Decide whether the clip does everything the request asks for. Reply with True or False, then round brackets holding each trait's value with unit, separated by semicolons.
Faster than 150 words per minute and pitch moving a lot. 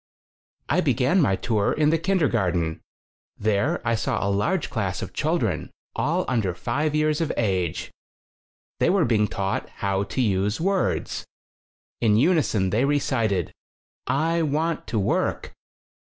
False (140 wpm; 7.6 semitones)